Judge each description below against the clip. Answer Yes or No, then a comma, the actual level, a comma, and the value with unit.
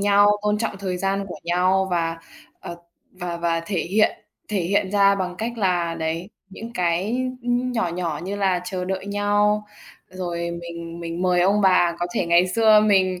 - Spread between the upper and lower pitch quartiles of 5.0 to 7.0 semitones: No, average, 2.9 semitones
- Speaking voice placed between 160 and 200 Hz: Yes, medium, 185 Hz